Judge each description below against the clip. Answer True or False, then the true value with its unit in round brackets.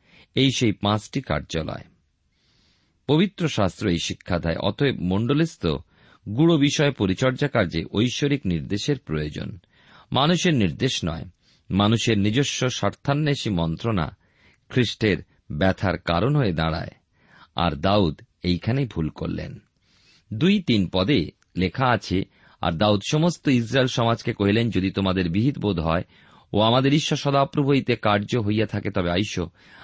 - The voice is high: False (105 Hz)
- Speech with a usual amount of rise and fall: False (6.5 semitones)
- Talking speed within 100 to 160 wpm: True (120 wpm)